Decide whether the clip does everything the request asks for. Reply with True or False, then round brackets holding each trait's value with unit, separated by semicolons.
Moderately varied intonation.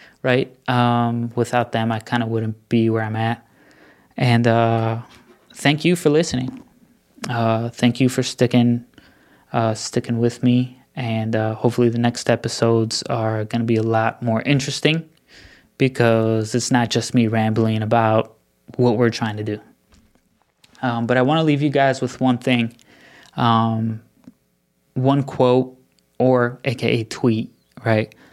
False (2.1 semitones)